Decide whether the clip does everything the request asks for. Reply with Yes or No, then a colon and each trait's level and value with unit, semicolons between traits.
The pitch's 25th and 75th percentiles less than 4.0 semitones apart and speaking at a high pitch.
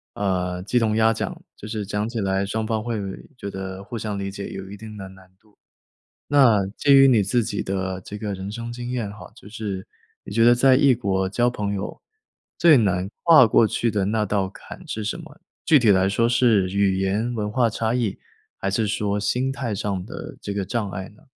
No: average, 3.1 semitones; low, 105 Hz